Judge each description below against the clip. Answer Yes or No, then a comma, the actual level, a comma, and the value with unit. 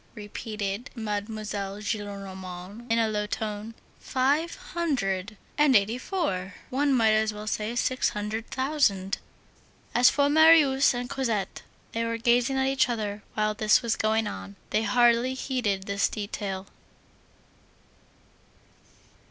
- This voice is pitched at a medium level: No, high, 220 Hz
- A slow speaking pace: Yes, slow, 125 wpm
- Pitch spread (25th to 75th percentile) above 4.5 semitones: No, average, 3.8 semitones